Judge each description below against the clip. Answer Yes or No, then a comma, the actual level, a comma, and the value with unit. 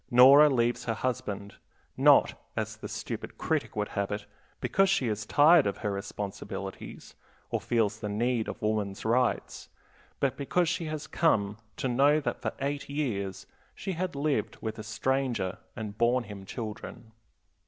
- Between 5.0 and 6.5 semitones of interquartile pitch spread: Yes, average, 5.3 semitones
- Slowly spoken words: No, average, 160 wpm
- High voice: No, low, 115 Hz